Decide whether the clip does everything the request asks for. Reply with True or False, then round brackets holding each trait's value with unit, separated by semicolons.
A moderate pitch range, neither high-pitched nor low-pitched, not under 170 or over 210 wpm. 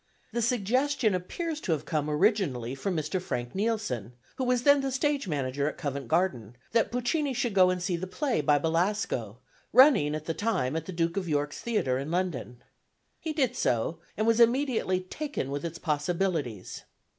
False (8.3 semitones; 180 Hz; 180 wpm)